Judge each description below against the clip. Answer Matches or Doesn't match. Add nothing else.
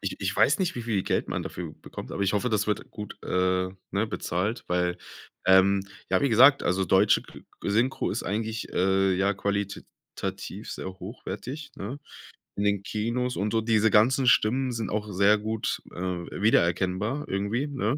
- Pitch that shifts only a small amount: Doesn't match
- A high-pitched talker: Doesn't match